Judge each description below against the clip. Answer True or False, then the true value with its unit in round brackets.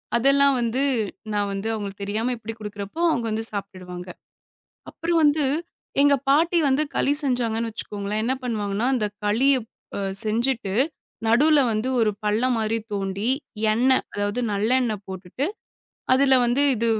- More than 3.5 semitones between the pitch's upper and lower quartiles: True (4.2 semitones)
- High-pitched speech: True (225 Hz)